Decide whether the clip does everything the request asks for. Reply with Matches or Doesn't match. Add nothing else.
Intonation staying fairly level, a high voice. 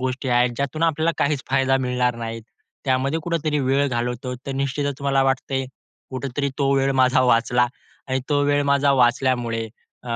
Doesn't match